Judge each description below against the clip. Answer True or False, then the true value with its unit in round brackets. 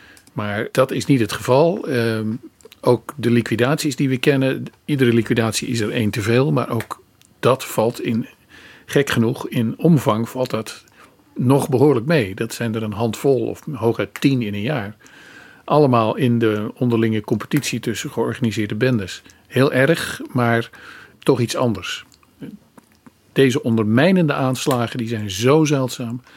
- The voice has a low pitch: True (120 Hz)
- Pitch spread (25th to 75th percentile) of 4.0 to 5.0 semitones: False (2.9 semitones)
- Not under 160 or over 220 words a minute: False (150 wpm)